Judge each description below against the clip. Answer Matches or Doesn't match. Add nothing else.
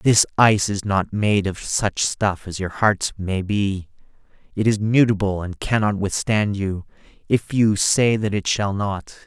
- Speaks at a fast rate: Doesn't match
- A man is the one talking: Matches